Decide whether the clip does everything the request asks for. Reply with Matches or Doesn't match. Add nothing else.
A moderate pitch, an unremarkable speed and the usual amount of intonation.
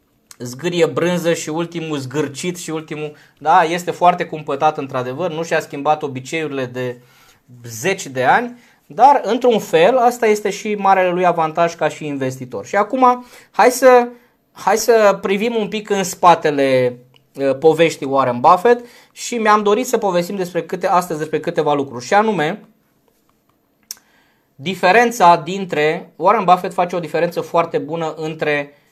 Matches